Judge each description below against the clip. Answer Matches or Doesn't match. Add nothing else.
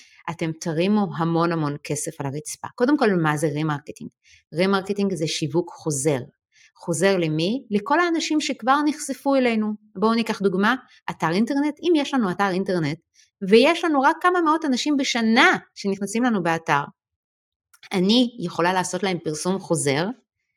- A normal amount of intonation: Doesn't match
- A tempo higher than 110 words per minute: Matches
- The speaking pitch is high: Matches